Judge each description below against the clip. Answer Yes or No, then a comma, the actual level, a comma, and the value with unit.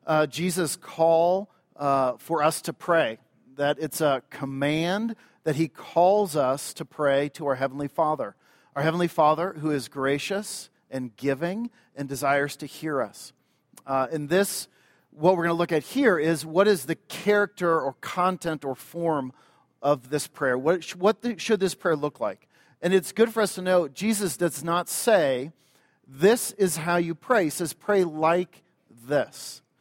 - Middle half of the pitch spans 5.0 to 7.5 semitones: No, average, 4.4 semitones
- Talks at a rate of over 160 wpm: Yes, average, 175 wpm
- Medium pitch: Yes, medium, 165 Hz